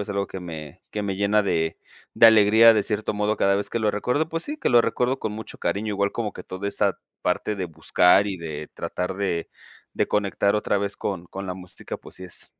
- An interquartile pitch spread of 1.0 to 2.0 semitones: No, narrow, 2.6 semitones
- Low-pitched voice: Yes, low, 100 Hz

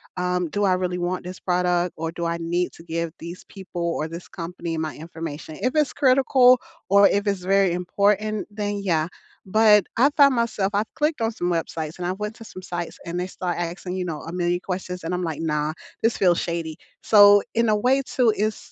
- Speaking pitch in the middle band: Yes, medium, 180 Hz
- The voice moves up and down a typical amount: Yes, average, 3.5 semitones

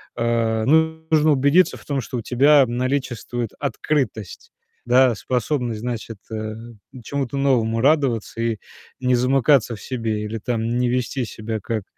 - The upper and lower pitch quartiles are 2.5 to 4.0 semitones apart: Yes, average, 3.4 semitones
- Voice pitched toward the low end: Yes, low, 125 Hz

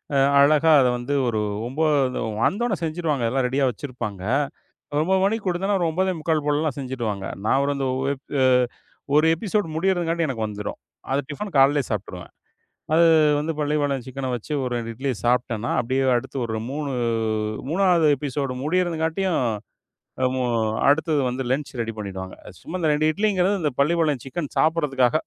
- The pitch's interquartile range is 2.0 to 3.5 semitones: No, average, 4.4 semitones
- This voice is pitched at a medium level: Yes, medium, 145 Hz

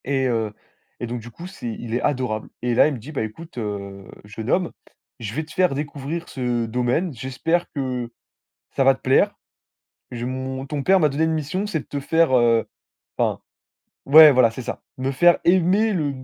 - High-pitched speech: No, low, 130 Hz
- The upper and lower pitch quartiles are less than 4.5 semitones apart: No, average, 4.9 semitones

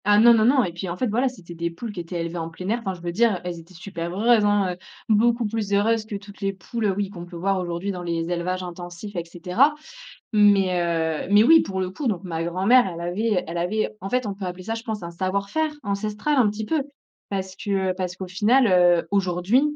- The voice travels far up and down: No, average, 3.6 semitones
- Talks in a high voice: Yes, high, 195 Hz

